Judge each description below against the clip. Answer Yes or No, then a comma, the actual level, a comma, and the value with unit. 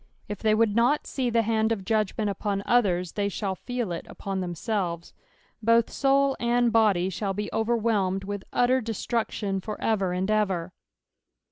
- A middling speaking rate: Yes, average, 160 wpm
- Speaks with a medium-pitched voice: No, high, 215 Hz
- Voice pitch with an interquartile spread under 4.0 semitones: Yes, average, 3.2 semitones